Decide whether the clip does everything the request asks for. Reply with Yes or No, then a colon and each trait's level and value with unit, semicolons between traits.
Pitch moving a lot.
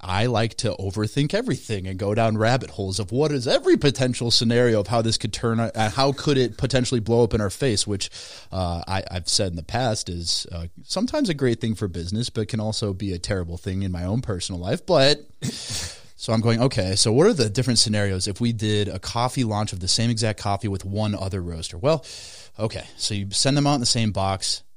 No: average, 4.0 semitones